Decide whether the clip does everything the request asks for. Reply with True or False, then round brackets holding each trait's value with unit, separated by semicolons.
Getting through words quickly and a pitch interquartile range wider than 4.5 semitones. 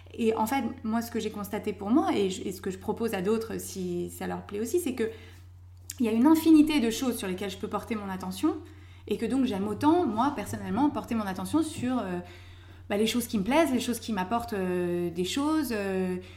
True (240 wpm; 5.0 semitones)